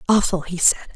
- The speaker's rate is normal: Yes, average, 190 wpm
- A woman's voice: Yes, female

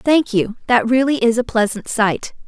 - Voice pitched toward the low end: No, high, 240 Hz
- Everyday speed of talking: Yes, average, 195 wpm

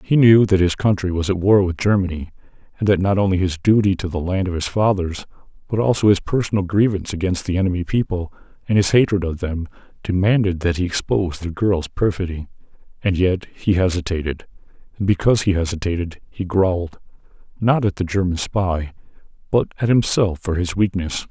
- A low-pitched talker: Yes, very low, 95 Hz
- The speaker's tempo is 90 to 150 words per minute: No, average, 175 wpm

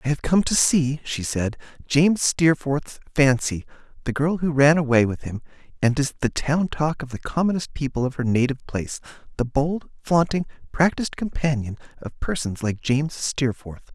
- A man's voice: Yes, male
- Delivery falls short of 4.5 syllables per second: No, 5.0 syllables/s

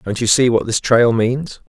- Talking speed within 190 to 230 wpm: No, fast, 240 wpm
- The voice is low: Yes, low, 120 Hz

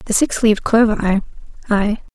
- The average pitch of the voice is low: No, high, 215 Hz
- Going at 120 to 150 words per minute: Yes, average, 140 wpm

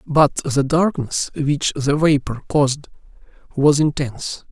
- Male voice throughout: Yes, male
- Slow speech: Yes, slow, 120 wpm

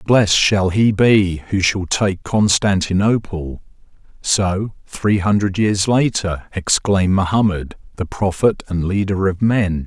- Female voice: No, male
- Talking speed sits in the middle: No, slow, 130 wpm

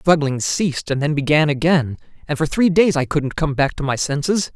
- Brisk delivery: Yes, fast, 235 wpm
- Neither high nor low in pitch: Yes, medium, 150 Hz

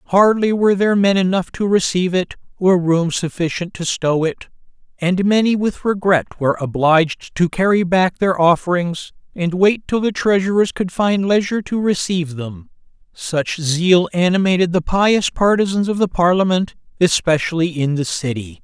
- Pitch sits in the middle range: Yes, medium, 180 Hz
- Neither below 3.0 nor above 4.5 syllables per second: No, 5.0 syllables/s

